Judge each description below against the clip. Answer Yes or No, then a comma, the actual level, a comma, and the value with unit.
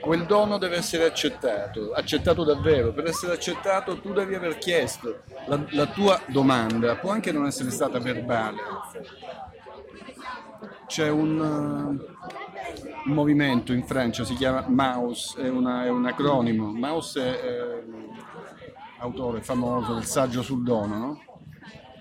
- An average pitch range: Yes, average, 4.2 semitones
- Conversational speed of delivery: Yes, average, 130 wpm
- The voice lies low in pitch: Yes, low, 130 Hz